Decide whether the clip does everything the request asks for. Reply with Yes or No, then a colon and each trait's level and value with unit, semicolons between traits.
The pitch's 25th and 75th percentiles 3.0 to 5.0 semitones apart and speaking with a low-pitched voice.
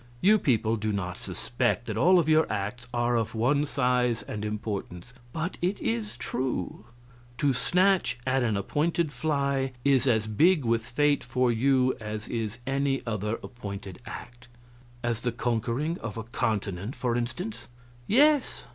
Yes: average, 4.1 semitones; low, 120 Hz